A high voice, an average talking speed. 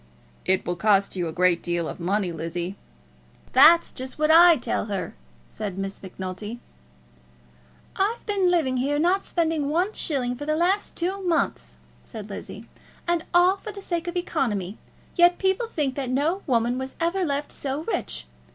Yes: very high, 280 Hz; average, 170 wpm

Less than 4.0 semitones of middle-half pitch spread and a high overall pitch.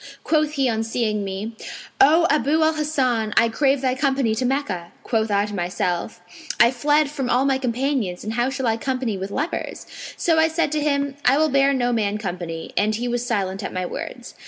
No: average, 4.9 semitones; high, 245 Hz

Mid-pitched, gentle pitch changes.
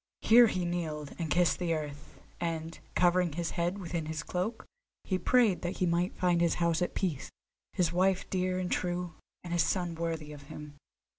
Yes: medium, 175 Hz; narrow, 2.0 semitones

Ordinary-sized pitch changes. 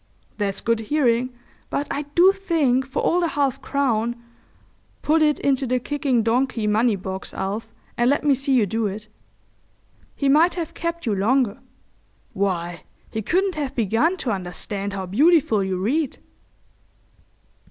No: wide, 5.7 semitones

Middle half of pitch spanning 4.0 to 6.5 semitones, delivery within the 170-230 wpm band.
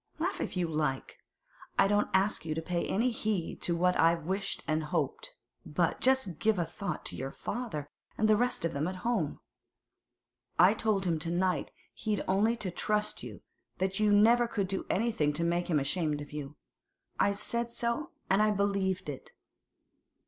Yes: average, 4.5 semitones; average, 185 wpm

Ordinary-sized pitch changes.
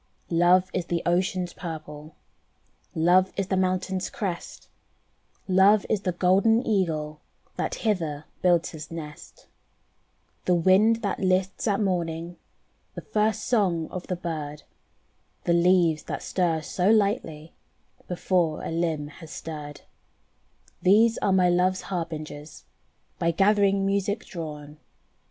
Yes: average, 3.1 semitones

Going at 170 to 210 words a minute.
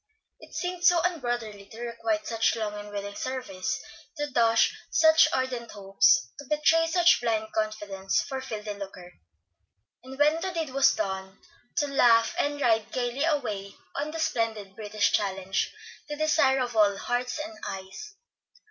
No: average, 155 wpm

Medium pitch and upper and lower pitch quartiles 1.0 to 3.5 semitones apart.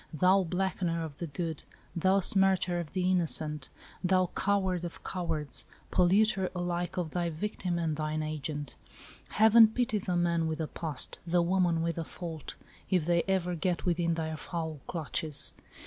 Yes: medium, 175 Hz; narrow, 2.5 semitones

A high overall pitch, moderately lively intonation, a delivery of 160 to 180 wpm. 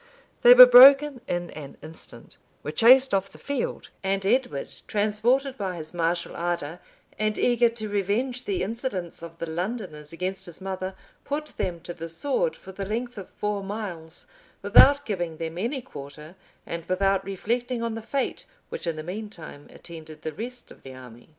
No: high, 195 Hz; wide, 6.1 semitones; average, 175 wpm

